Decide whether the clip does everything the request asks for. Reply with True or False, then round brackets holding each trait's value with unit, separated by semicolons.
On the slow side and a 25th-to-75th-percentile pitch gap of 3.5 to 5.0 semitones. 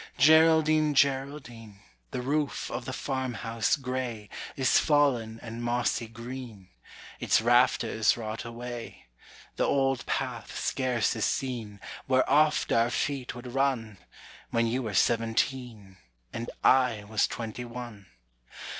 False (120 wpm; 2.8 semitones)